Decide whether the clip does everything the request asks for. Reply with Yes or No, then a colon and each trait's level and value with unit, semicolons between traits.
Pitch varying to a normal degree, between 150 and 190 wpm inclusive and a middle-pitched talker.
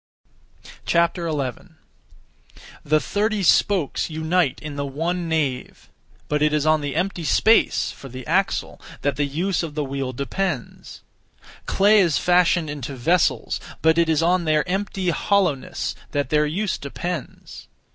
No: average, 3.8 semitones; average, 140 wpm; medium, 160 Hz